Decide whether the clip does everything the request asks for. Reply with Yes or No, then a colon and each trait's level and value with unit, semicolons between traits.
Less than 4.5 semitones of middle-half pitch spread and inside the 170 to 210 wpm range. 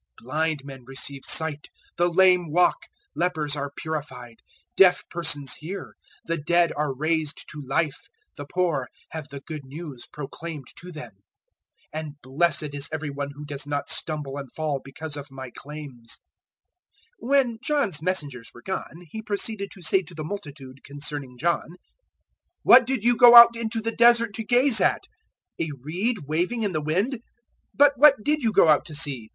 No: average, 5.0 semitones; average, 175 wpm